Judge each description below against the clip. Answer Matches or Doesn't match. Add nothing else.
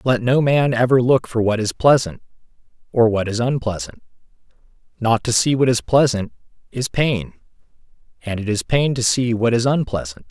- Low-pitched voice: Matches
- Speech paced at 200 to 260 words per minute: Doesn't match